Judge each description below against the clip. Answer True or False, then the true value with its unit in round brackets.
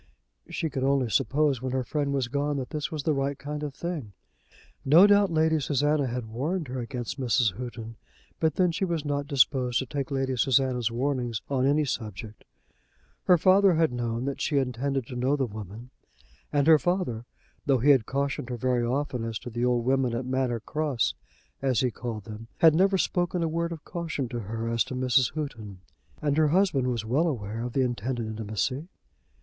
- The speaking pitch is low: True (130 Hz)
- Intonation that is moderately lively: True (3.8 semitones)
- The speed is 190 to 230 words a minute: True (200 wpm)